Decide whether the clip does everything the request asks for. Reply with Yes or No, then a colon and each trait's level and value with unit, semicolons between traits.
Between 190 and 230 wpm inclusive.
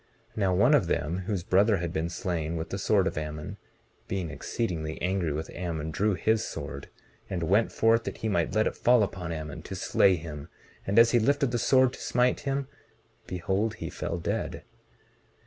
Yes: average, 195 wpm